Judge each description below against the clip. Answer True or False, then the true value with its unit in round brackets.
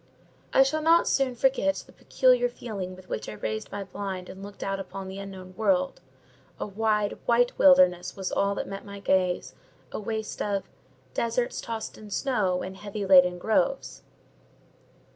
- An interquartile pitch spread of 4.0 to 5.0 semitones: True (4.5 semitones)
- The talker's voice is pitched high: True (200 Hz)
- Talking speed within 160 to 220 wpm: True (165 wpm)